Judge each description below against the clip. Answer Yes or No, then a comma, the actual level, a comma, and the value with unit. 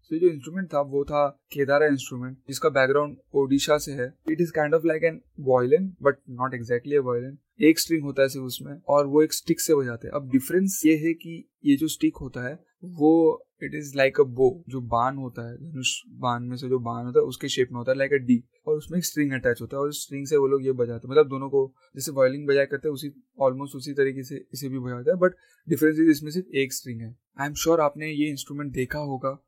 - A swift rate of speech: Yes, fast, 240 wpm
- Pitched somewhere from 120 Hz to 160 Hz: Yes, medium, 140 Hz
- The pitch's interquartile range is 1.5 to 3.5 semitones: Yes, average, 3.0 semitones